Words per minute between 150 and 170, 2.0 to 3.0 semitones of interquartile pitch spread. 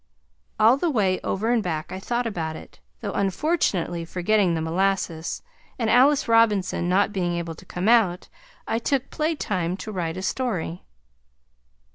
No: average, 155 wpm; average, 4.7 semitones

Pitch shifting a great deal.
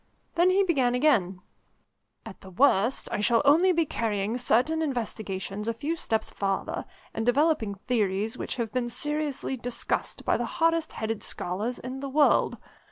Yes: wide, 5.8 semitones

